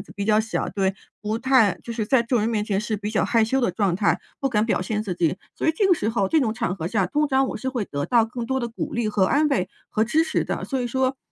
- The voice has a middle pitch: No, high, 225 Hz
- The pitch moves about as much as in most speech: Yes, average, 4.2 semitones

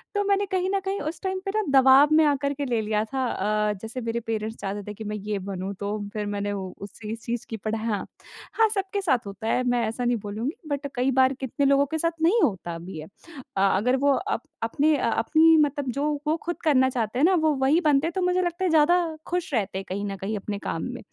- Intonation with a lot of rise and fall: Yes, wide, 6.9 semitones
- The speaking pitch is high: Yes, very high, 260 Hz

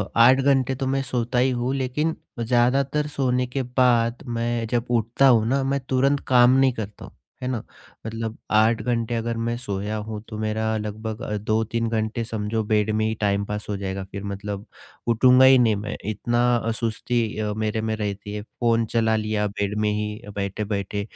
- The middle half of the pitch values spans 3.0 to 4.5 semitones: No, narrow, 2.6 semitones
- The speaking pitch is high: No, low, 115 Hz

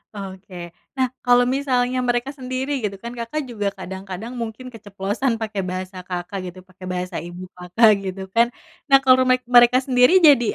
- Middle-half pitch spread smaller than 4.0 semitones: No, average, 4.9 semitones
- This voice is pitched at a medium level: No, high, 225 Hz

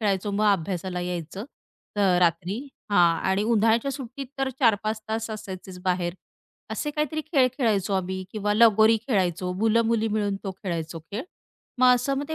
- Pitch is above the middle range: Yes, high, 205 Hz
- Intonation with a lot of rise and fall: No, average, 3.7 semitones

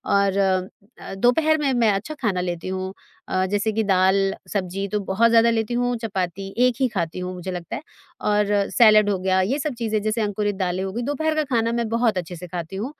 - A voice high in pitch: Yes, high, 205 Hz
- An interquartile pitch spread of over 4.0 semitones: No, average, 3.6 semitones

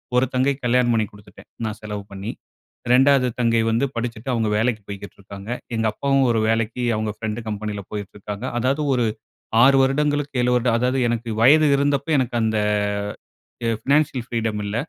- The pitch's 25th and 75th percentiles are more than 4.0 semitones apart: No, average, 3.5 semitones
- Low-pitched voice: Yes, low, 120 Hz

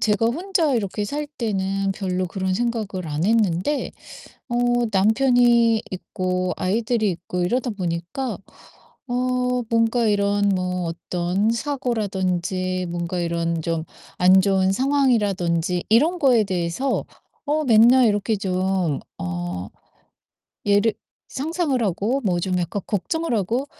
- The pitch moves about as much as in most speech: Yes, average, 4.9 semitones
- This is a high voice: Yes, high, 200 Hz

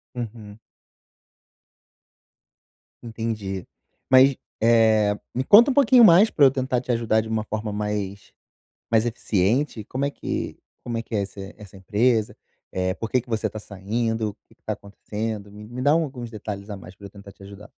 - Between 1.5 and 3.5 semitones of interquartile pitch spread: Yes, average, 3.1 semitones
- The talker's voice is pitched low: Yes, low, 110 Hz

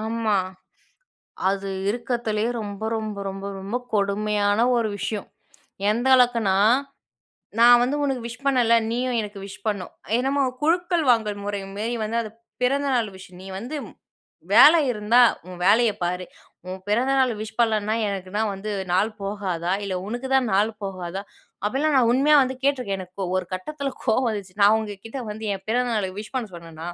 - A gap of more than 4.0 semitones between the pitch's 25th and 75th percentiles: No, average, 3.7 semitones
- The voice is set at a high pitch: Yes, high, 215 Hz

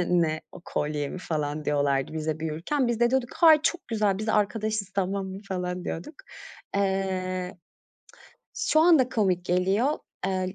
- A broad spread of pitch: No, average, 4.2 semitones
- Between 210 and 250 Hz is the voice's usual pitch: No, high, 190 Hz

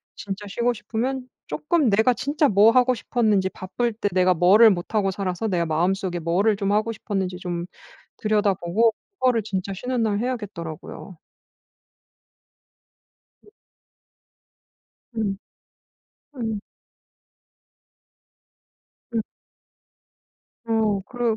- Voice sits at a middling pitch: No, high, 210 Hz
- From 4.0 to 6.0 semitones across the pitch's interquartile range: No, average, 3.5 semitones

